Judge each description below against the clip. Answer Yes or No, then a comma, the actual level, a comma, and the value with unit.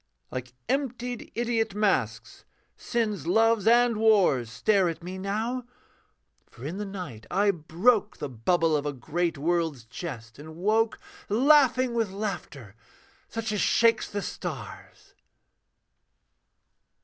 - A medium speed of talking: No, slow, 125 wpm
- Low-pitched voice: No, high, 195 Hz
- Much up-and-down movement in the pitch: Yes, wide, 6.8 semitones